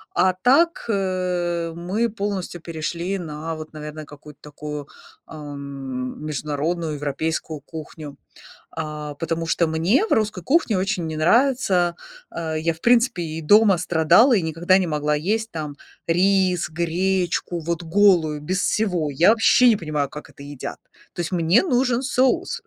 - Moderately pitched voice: Yes, medium, 170 Hz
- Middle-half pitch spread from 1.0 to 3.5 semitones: No, average, 4.1 semitones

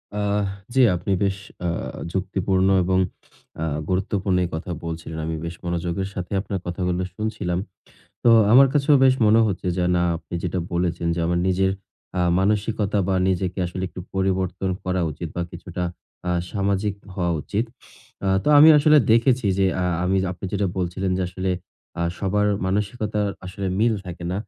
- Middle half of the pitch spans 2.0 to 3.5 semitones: Yes, narrow, 2.6 semitones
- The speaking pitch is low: Yes, very low, 95 Hz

